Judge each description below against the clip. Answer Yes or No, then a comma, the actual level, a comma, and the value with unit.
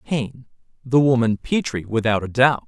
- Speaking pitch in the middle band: No, low, 120 Hz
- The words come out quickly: No, slow, 135 wpm